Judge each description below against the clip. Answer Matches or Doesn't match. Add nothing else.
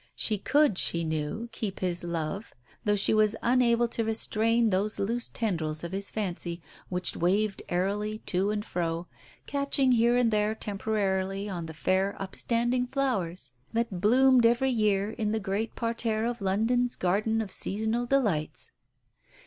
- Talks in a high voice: Matches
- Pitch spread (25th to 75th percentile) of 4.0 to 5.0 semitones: Doesn't match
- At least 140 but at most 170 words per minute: Matches